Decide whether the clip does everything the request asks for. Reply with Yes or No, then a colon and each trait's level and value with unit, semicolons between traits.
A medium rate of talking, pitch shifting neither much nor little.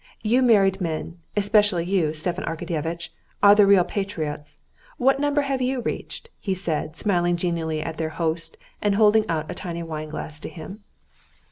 Yes: average, 165 wpm; average, 4.2 semitones